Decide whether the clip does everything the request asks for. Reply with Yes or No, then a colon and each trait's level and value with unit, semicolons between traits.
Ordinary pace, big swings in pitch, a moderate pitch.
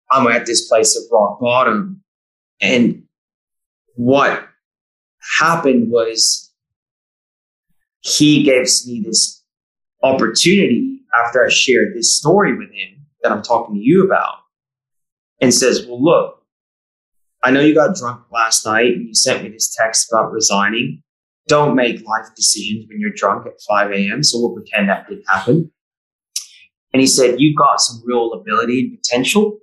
No: average, 150 wpm; wide, 7.5 semitones; low, 130 Hz